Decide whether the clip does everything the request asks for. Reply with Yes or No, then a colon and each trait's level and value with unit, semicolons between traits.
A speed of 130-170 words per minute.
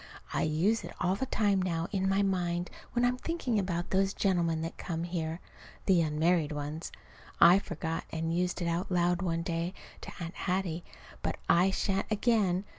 No: average, 180 wpm